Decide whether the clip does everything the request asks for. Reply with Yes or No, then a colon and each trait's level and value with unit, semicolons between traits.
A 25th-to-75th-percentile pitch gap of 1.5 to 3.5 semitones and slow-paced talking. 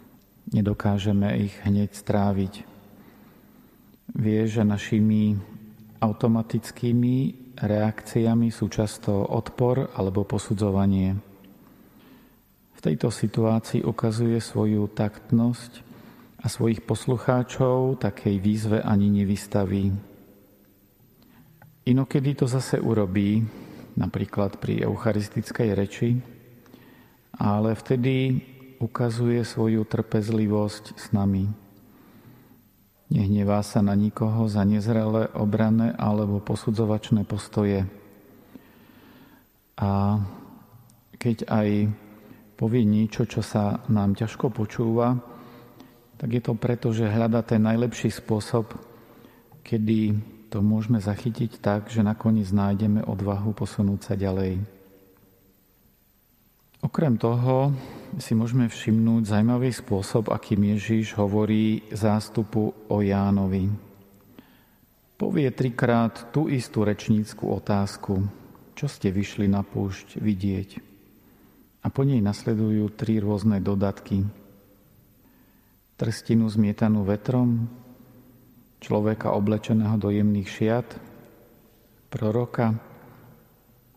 Yes: narrow, 2.6 semitones; slow, 90 wpm